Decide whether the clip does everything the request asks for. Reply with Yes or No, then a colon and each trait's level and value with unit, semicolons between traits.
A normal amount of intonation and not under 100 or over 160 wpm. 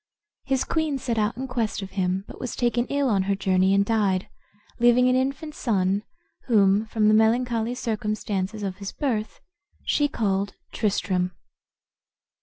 Yes: average, 4.1 semitones; average, 155 wpm